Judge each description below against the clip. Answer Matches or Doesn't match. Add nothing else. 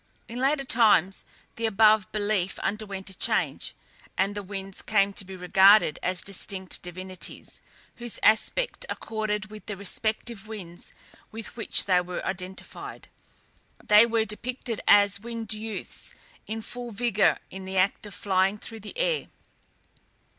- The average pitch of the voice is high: Matches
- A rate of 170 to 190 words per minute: Doesn't match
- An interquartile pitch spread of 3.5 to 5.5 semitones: Doesn't match